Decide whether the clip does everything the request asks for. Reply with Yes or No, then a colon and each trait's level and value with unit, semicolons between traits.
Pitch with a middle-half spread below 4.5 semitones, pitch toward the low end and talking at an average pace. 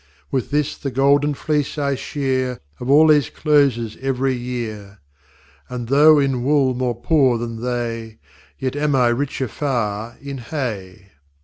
Yes: average, 3.1 semitones; low, 130 Hz; average, 145 wpm